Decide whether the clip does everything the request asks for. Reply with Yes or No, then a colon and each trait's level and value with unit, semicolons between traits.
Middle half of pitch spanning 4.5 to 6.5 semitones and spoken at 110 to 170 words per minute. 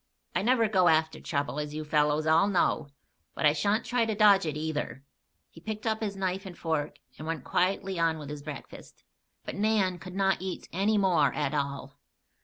No: average, 4.8 semitones; average, 200 wpm